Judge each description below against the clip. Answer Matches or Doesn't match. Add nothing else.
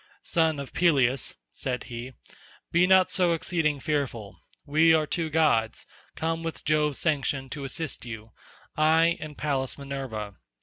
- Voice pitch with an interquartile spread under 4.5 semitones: Matches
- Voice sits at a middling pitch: Matches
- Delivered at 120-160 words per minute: Matches